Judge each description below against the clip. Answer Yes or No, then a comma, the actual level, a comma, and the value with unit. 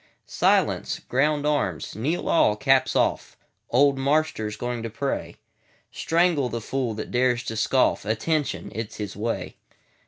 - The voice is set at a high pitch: No, low, 125 Hz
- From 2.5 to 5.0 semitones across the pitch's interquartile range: Yes, average, 4.5 semitones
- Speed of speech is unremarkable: No, slow, 120 wpm